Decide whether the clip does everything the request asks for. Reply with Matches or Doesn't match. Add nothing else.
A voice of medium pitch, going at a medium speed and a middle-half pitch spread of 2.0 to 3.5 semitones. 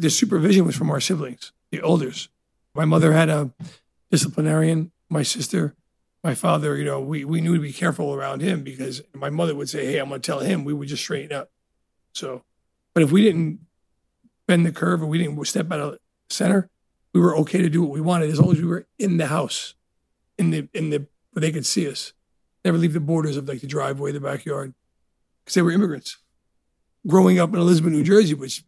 Doesn't match